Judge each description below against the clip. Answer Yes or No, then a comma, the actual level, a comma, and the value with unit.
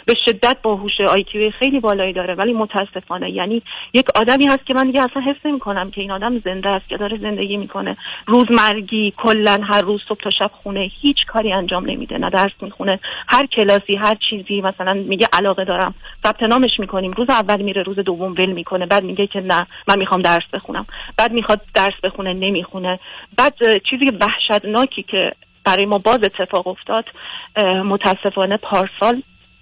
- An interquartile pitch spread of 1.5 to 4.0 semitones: Yes, average, 2.9 semitones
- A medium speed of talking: No, fast, 175 wpm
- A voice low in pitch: No, high, 205 Hz